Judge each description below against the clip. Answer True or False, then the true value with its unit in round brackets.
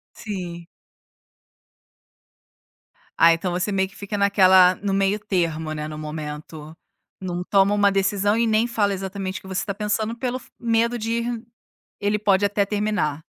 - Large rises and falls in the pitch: False (2.8 semitones)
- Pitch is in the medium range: False (195 Hz)